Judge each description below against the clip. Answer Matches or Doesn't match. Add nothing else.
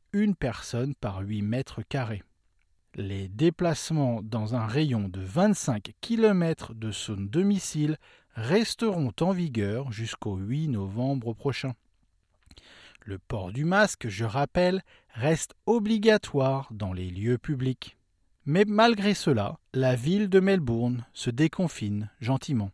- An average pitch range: Doesn't match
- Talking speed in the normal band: Doesn't match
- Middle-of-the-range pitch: Doesn't match